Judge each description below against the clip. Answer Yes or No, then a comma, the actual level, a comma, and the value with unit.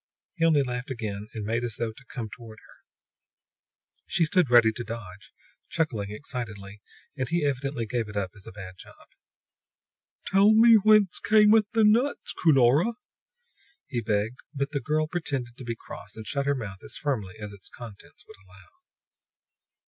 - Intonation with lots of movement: Yes, wide, 6.5 semitones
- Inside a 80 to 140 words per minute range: No, average, 170 wpm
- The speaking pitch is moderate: No, low, 120 Hz